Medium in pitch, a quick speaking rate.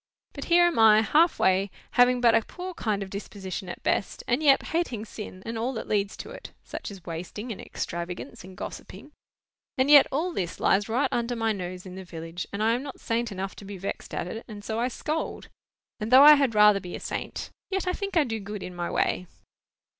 No: high, 220 Hz; fast, 225 wpm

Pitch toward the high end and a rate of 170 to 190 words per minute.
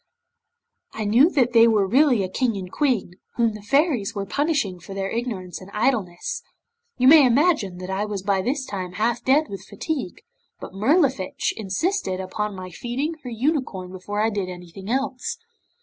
Yes: high, 220 Hz; average, 175 wpm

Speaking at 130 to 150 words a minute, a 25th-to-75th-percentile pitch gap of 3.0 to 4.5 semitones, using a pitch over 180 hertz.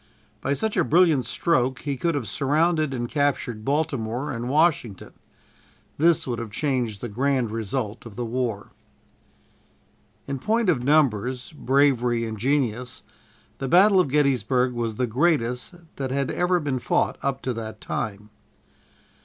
No: average, 145 wpm; average, 4.0 semitones; low, 130 Hz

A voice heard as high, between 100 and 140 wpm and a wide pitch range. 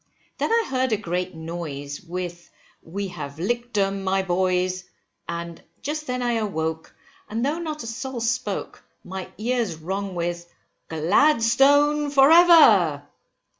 Yes: high, 195 Hz; slow, 135 wpm; wide, 6.7 semitones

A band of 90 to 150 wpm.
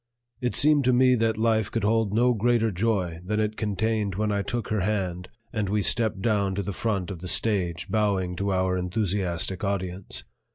No: average, 195 wpm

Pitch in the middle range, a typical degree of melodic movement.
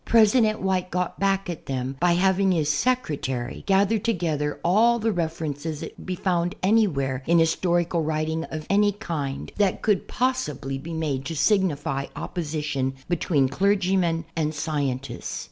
Yes: medium, 170 Hz; average, 4.7 semitones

